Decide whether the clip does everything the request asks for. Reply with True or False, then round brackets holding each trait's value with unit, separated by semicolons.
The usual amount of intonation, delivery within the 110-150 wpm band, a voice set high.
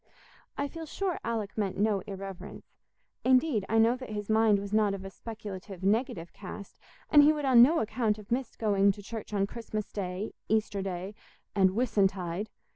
False (3.0 semitones; 180 wpm; 210 Hz)